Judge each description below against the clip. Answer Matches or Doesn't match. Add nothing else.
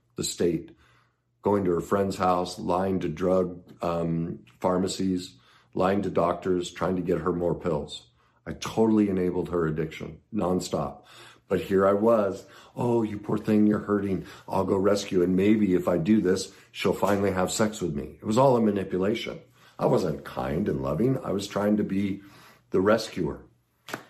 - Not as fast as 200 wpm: Matches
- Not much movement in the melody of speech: Matches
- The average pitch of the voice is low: Matches